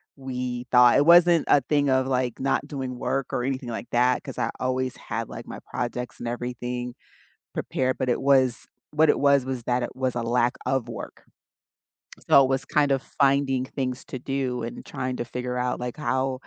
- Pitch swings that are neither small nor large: No, narrow, 1.5 semitones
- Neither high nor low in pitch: No, low, 130 Hz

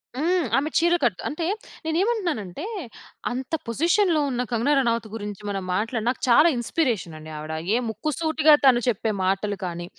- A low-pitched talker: No, high, 245 Hz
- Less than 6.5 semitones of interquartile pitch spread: No, wide, 7.3 semitones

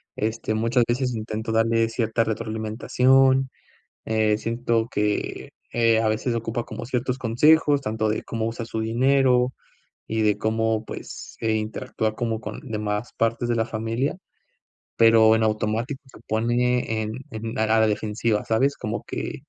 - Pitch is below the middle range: Yes, low, 115 Hz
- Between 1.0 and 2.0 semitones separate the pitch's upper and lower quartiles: Yes, narrow, 1.7 semitones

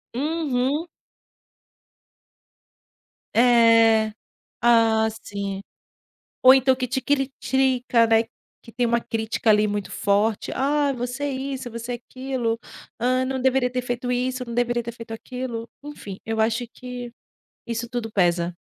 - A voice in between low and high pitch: No, high, 240 Hz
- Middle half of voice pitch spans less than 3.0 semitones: Yes, narrow, 2.4 semitones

